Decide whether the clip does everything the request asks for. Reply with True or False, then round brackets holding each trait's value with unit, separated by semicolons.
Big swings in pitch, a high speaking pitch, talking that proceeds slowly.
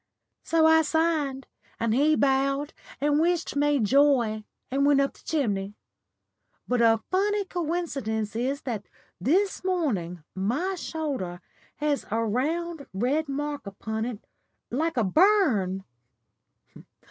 True (6.2 semitones; 280 Hz; 125 wpm)